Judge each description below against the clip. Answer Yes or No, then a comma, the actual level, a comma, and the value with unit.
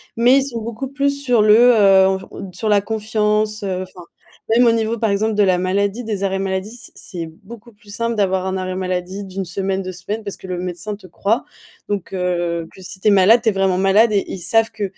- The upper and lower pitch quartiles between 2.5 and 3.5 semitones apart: Yes, average, 2.8 semitones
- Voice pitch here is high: Yes, high, 200 Hz